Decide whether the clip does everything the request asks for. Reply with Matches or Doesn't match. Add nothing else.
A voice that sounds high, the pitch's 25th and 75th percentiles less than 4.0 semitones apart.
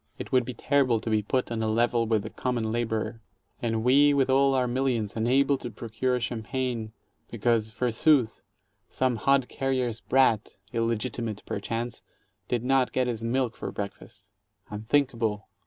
Doesn't match